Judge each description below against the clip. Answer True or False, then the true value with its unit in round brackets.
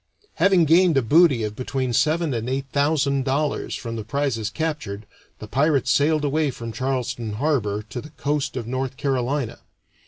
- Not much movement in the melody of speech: False (3.9 semitones)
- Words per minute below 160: False (165 wpm)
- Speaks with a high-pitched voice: False (135 Hz)